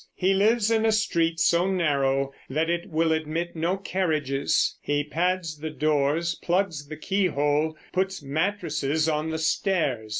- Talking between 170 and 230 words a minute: No, average, 145 wpm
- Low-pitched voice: No, medium, 160 Hz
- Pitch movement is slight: No, average, 3.6 semitones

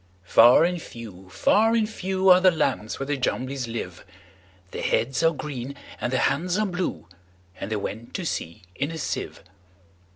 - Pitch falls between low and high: No, low, 130 Hz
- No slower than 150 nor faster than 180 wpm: Yes, average, 160 wpm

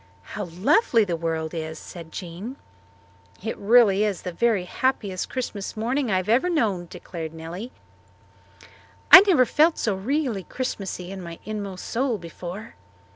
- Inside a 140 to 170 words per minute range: Yes, average, 145 wpm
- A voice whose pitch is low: No, high, 200 Hz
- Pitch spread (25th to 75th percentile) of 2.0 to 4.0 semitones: No, wide, 5.5 semitones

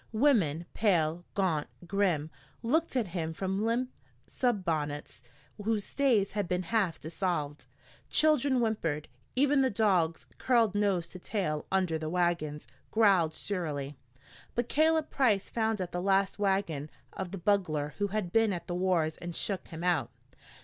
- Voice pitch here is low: No, high, 190 Hz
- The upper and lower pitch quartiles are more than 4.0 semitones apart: Yes, average, 5.2 semitones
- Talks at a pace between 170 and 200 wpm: No, average, 150 wpm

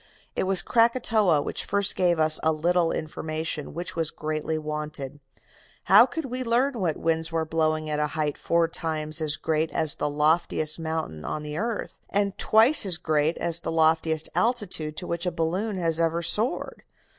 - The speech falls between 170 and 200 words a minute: Yes, average, 180 wpm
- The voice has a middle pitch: Yes, medium, 160 Hz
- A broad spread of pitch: No, average, 3.1 semitones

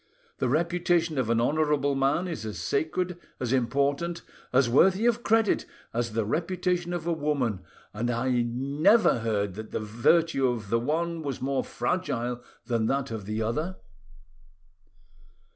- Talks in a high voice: No, medium, 140 Hz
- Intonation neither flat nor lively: No, wide, 6.4 semitones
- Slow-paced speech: No, average, 150 wpm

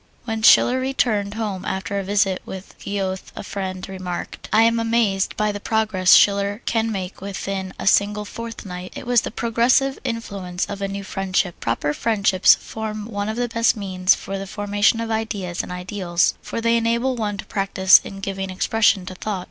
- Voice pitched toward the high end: Yes, high, 200 Hz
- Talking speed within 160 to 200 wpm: Yes, average, 185 wpm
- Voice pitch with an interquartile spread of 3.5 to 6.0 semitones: No, average, 2.7 semitones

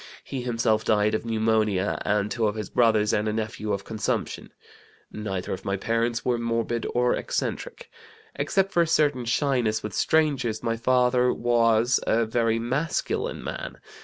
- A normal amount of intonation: No, narrow, 2.3 semitones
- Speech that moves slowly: No, average, 160 wpm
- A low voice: Yes, low, 115 Hz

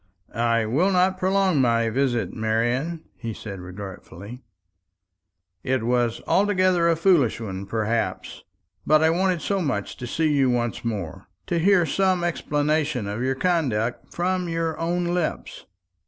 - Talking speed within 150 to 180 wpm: No, average, 140 wpm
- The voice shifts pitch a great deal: Yes, wide, 7.0 semitones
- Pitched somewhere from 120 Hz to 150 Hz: Yes, medium, 140 Hz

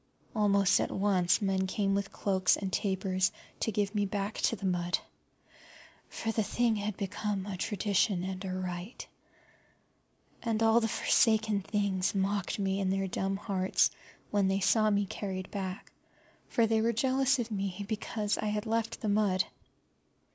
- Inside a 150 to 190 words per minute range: Yes, average, 160 wpm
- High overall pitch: Yes, high, 200 Hz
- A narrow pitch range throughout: Yes, narrow, 2.1 semitones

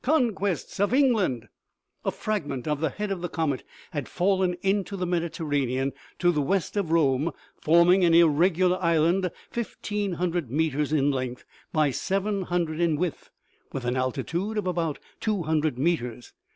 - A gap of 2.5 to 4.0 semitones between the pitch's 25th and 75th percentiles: No, average, 4.5 semitones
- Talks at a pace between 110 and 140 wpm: No, average, 160 wpm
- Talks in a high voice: No, medium, 170 Hz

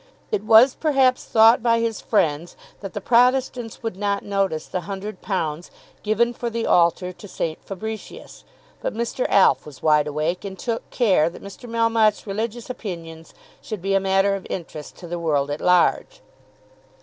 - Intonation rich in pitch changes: No, average, 4.8 semitones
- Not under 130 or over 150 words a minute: No, average, 165 wpm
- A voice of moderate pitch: No, high, 200 Hz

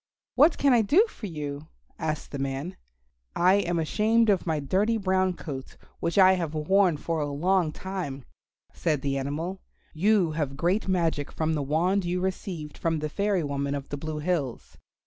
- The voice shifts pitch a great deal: No, average, 4.3 semitones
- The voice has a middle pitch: Yes, medium, 165 Hz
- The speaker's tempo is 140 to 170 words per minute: No, average, 180 wpm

